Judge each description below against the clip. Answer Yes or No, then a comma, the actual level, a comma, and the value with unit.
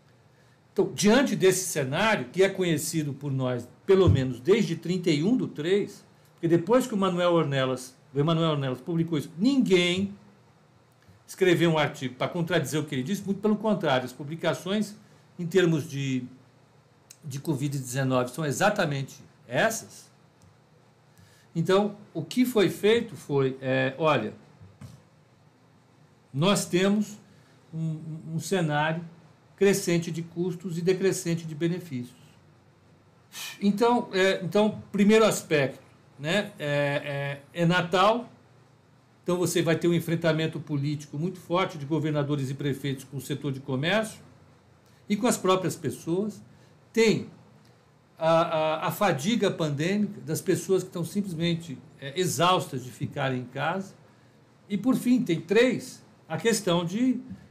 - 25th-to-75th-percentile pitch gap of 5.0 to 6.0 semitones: Yes, wide, 5.4 semitones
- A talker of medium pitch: Yes, medium, 165 Hz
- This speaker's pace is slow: No, average, 135 wpm